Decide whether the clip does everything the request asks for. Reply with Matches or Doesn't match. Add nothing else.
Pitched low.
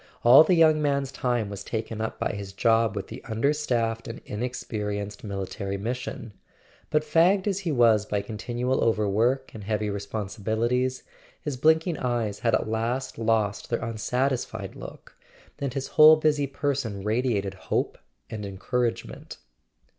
Matches